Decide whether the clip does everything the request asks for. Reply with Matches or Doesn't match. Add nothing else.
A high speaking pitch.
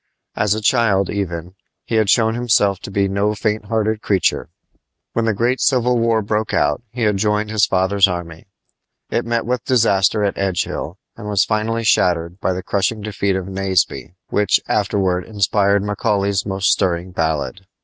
Doesn't match